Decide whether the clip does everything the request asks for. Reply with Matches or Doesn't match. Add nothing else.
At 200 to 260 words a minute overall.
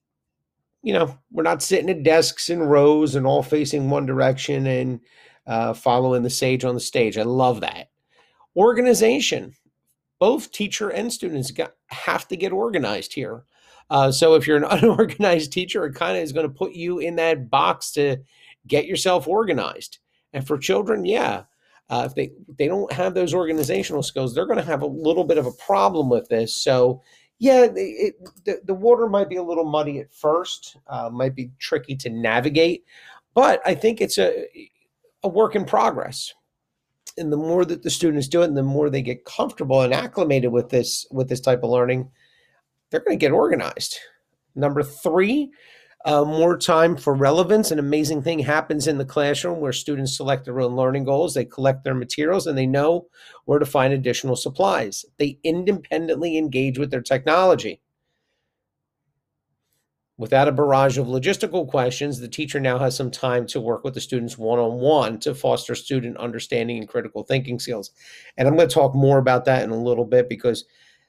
Doesn't match